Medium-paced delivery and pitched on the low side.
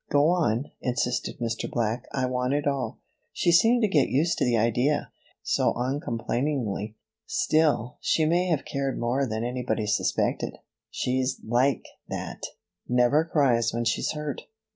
Yes: average, 150 wpm; low, 130 Hz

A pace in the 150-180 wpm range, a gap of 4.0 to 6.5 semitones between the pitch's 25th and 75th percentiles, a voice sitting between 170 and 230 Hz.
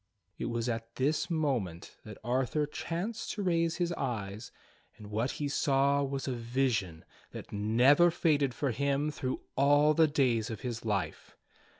No: average, 160 wpm; average, 4.6 semitones; low, 135 Hz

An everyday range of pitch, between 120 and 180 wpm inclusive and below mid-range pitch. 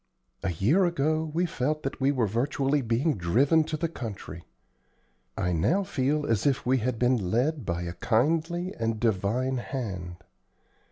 No: wide, 6.0 semitones; average, 160 wpm; low, 130 Hz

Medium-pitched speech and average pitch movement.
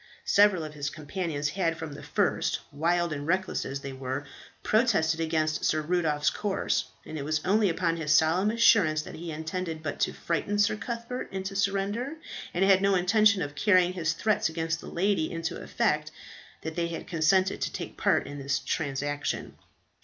Yes: medium, 165 Hz; average, 3.9 semitones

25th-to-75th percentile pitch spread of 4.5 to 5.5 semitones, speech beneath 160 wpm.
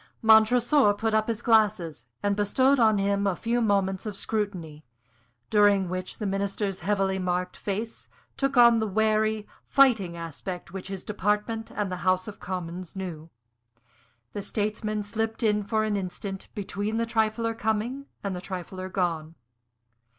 No: average, 2.8 semitones; average, 150 wpm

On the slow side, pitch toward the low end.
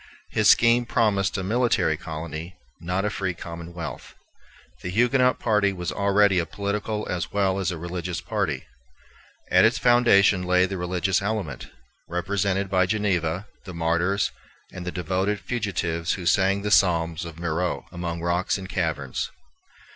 No: average, 145 wpm; very low, 95 Hz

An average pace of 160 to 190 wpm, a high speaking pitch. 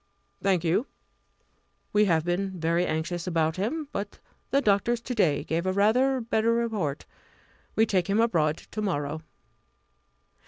No: average, 145 wpm; high, 195 Hz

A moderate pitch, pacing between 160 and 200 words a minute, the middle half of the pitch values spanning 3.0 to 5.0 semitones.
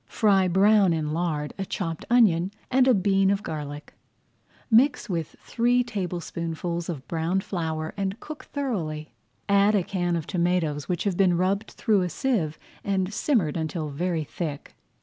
Yes: medium, 180 Hz; average, 165 wpm; average, 3.8 semitones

